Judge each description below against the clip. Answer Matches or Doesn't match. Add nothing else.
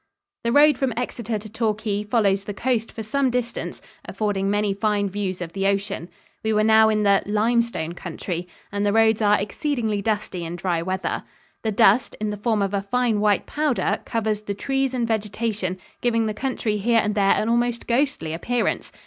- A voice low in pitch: Doesn't match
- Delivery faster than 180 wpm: Matches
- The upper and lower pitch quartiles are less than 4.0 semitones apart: Matches